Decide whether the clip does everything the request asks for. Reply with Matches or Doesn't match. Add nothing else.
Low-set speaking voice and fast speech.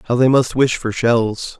Matches